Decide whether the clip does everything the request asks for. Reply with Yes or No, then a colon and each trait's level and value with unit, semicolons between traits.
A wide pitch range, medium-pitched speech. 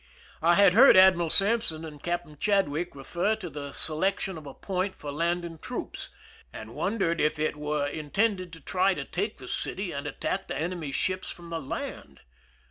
No: average, 3.8 semitones; medium, 170 Hz